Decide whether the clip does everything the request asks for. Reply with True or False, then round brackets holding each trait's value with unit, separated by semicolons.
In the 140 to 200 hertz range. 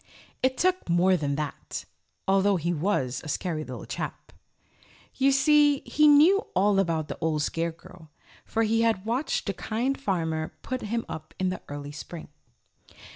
True (190 Hz)